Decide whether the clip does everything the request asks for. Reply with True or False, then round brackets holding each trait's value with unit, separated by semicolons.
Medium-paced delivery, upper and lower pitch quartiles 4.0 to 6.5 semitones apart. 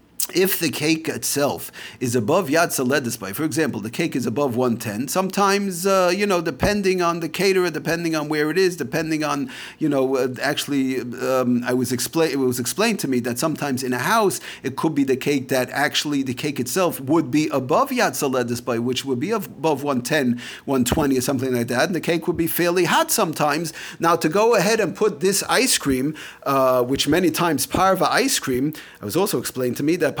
False (210 wpm; 4.7 semitones)